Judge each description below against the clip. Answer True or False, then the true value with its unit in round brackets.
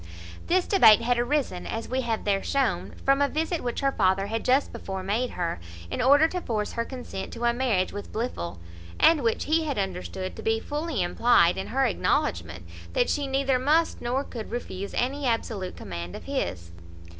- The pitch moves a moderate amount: False (6.0 semitones)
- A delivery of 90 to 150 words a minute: False (190 wpm)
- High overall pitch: True (235 Hz)